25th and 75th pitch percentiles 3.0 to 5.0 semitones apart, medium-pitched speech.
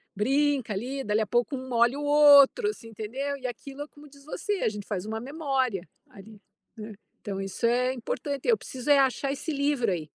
No: average, 4.4 semitones; very high, 260 Hz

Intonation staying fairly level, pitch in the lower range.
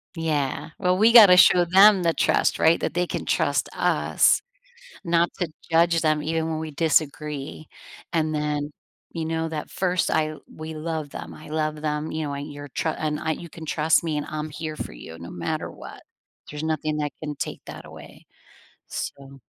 No: narrow, 1.7 semitones; medium, 155 Hz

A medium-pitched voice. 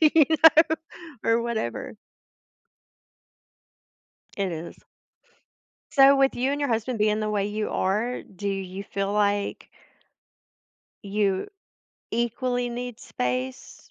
No: high, 215 Hz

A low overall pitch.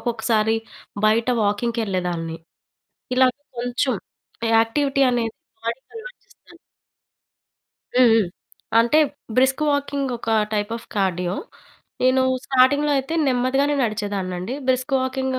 No: high, 245 Hz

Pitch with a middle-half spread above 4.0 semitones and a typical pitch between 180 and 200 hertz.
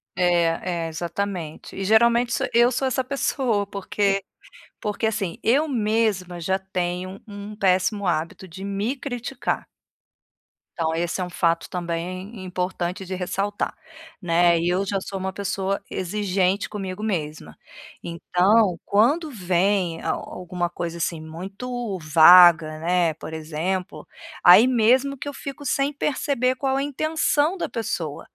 Yes: average, 4.4 semitones; high, 190 Hz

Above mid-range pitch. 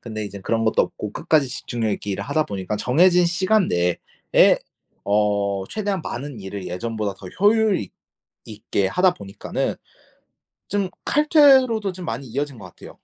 No: low, 120 Hz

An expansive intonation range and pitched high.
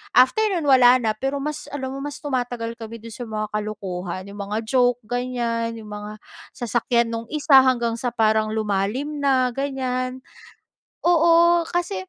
No: average, 3.7 semitones; high, 245 Hz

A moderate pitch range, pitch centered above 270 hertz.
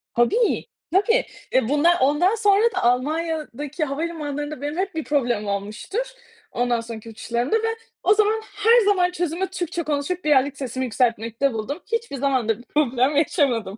No: wide, 6.6 semitones; very high, 290 Hz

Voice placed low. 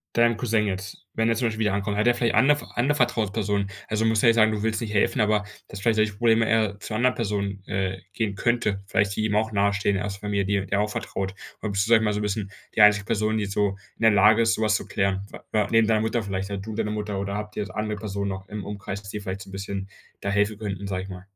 Yes: low, 105 Hz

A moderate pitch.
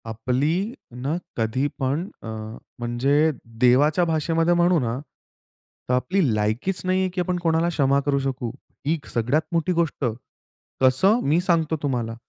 Yes: medium, 145 Hz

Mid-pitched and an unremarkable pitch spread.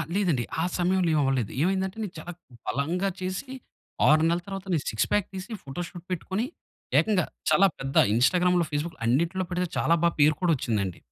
Yes: medium, 175 Hz; average, 4.3 semitones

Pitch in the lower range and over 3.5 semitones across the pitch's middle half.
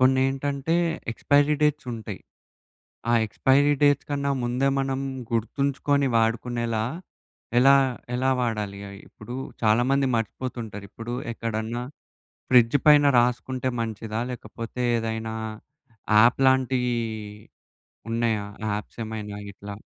No: low, 120 Hz; average, 3.1 semitones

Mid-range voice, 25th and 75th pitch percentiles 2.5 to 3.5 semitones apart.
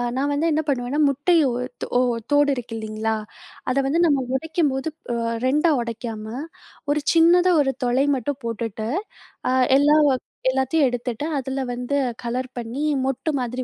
No: very high, 265 Hz; average, 3.2 semitones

